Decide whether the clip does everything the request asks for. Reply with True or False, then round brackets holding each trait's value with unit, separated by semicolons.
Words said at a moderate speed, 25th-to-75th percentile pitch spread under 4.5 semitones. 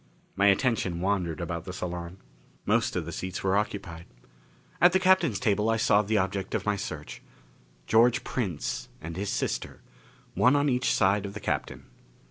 True (170 wpm; 3.8 semitones)